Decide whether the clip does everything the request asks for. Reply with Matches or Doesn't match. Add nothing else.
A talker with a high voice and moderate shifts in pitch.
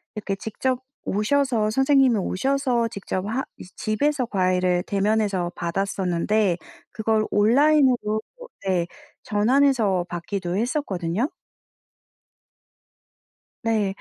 Matches